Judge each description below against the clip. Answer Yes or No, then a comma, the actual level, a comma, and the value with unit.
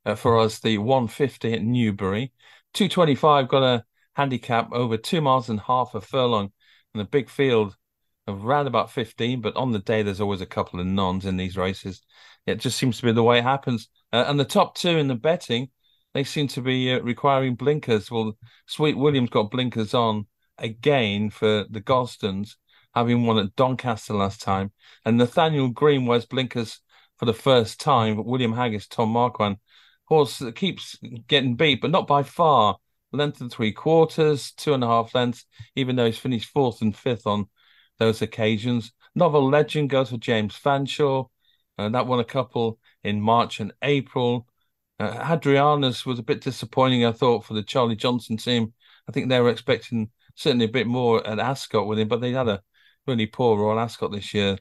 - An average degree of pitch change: Yes, average, 3.4 semitones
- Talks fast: No, average, 195 wpm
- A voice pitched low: Yes, low, 120 Hz